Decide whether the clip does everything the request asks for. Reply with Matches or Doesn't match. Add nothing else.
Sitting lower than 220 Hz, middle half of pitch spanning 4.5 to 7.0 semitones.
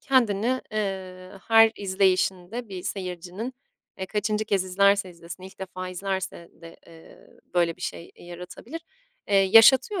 Doesn't match